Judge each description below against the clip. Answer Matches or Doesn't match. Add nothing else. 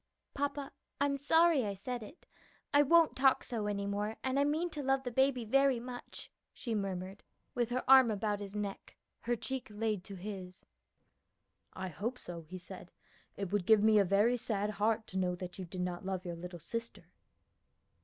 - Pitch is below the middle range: Doesn't match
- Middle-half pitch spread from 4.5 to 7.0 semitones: Matches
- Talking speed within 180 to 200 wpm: Matches